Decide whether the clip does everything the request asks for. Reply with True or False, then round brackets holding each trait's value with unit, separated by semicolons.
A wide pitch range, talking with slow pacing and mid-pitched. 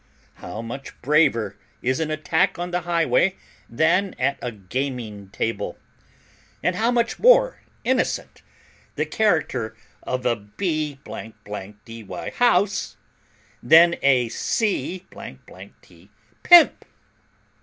True (7.9 semitones; 105 wpm; 150 Hz)